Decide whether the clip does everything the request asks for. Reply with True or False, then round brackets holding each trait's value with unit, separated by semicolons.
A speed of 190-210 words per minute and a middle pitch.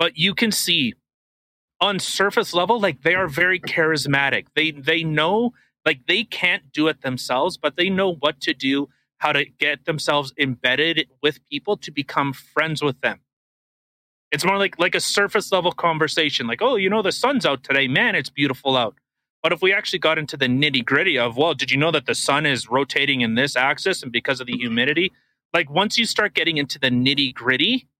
True (200 wpm; 155 Hz)